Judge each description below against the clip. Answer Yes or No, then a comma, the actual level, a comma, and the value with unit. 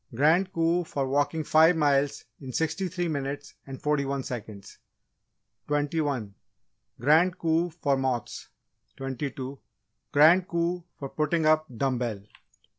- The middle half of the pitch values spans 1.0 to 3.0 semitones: No, average, 3.4 semitones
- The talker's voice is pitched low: No, medium, 145 Hz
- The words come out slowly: Yes, slow, 130 wpm